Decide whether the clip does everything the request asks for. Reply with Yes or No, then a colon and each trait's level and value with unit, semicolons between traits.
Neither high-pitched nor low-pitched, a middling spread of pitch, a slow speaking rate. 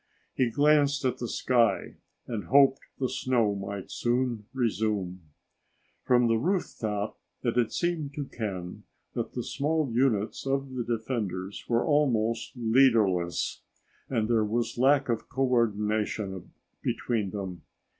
No: low, 115 Hz; average, 4.0 semitones; slow, 130 wpm